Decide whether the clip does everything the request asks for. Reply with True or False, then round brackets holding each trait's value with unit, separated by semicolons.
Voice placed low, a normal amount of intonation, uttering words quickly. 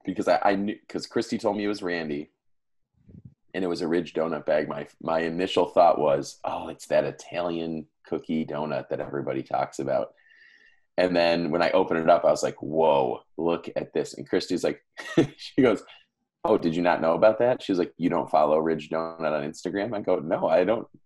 False (85 Hz; 2.0 semitones; 210 wpm)